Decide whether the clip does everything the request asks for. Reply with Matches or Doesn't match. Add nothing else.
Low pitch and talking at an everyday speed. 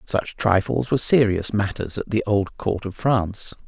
Matches